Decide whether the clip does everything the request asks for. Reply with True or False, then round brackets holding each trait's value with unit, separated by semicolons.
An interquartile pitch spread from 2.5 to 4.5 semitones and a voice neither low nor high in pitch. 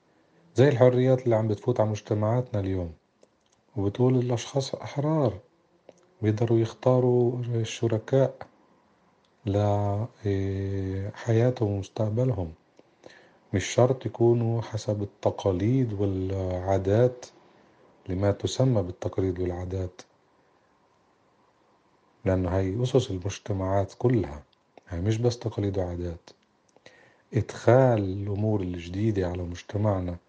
False (4.1 semitones; 105 Hz)